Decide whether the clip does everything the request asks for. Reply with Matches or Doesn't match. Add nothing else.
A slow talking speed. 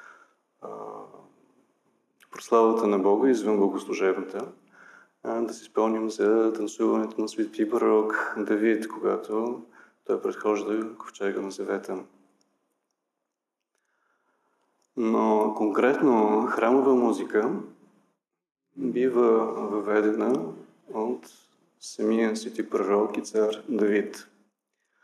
Matches